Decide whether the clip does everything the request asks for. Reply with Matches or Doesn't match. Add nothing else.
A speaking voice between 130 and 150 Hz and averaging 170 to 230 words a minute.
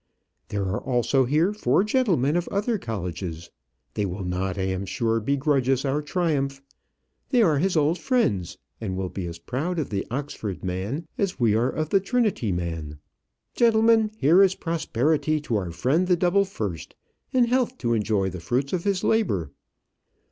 Matches